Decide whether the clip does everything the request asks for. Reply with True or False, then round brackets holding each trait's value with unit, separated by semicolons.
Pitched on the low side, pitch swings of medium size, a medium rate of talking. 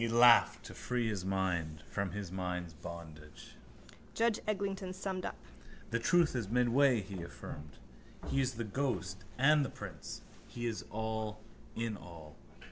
False (110 Hz; 6.2 semitones; 150 wpm)